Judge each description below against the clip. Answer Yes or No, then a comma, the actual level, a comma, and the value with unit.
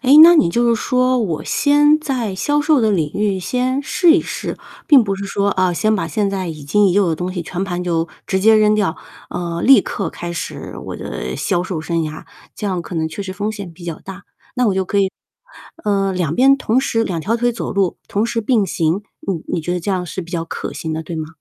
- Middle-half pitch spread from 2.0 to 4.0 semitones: No, average, 4.8 semitones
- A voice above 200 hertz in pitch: No, high, 195 Hz